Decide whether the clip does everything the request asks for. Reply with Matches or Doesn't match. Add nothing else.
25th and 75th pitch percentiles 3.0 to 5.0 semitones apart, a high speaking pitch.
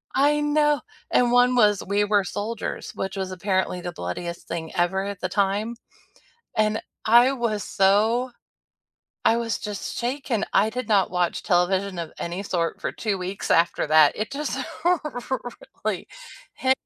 Matches